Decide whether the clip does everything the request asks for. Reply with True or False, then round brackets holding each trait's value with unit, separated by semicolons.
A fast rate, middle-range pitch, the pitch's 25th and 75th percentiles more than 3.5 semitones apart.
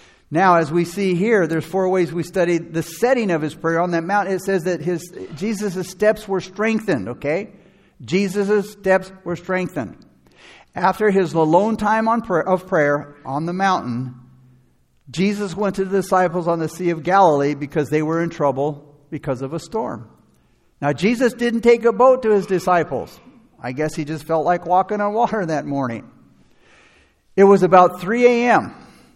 False (175 wpm; 180 Hz; 4.0 semitones)